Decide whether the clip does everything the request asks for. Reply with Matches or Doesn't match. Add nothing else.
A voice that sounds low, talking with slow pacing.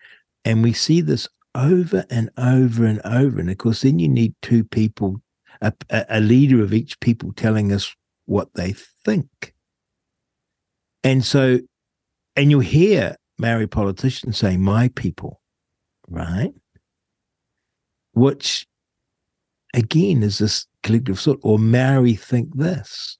Matches